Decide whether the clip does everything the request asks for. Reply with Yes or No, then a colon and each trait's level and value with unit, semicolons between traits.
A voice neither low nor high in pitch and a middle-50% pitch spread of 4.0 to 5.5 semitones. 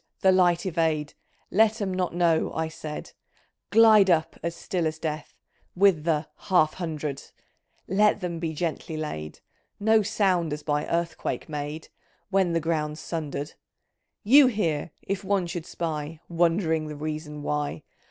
No: medium, 165 Hz; average, 3.3 semitones